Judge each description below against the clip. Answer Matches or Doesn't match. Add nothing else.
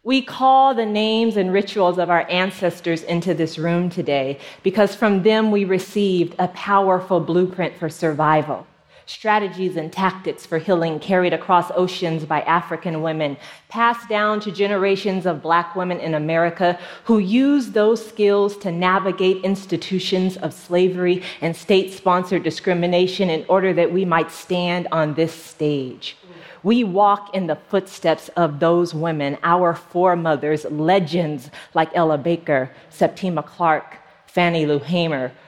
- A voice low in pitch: Doesn't match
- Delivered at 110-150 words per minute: Matches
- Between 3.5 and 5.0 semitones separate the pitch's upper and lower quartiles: Doesn't match